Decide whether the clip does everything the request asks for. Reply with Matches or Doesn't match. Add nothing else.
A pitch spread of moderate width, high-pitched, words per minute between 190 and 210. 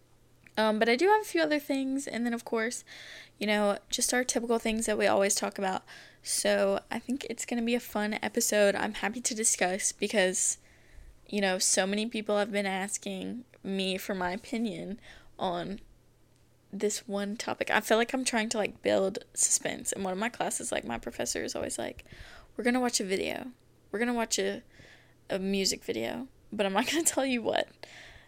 Matches